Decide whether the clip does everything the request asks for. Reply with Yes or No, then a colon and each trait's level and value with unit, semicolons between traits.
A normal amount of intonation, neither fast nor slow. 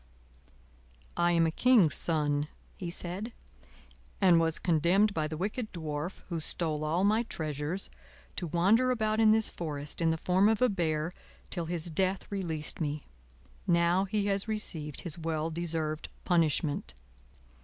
Yes: average, 3.9 semitones; average, 150 wpm